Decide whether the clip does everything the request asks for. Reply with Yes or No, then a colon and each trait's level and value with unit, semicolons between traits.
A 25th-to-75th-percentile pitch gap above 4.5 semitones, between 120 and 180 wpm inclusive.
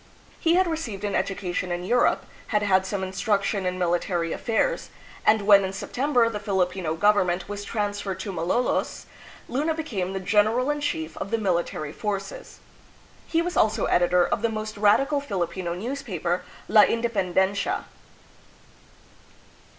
No: average, 3.9 semitones; average, 160 wpm